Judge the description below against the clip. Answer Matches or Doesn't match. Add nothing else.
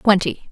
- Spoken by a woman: Matches